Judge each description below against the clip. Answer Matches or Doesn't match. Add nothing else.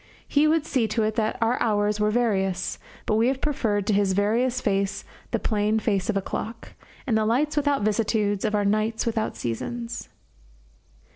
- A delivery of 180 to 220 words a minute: Matches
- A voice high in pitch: Matches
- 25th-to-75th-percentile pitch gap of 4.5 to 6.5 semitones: Doesn't match